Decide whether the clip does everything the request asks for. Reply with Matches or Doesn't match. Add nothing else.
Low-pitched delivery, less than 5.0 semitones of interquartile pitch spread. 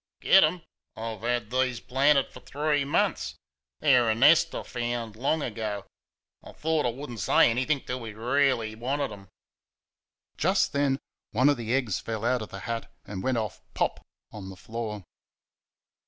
Matches